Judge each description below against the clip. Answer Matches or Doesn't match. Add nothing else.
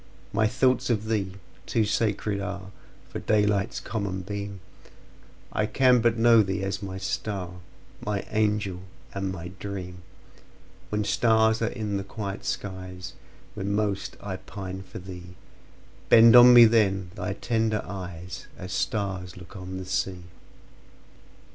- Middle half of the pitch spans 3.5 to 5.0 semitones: Doesn't match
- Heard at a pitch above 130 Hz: Doesn't match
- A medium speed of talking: Doesn't match